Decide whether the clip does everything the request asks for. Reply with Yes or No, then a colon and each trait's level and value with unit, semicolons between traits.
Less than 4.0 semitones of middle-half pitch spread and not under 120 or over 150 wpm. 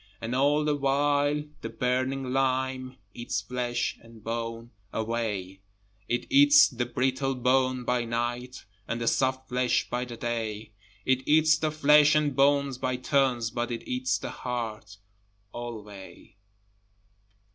Yes: narrow, 2.5 semitones; slow, 135 wpm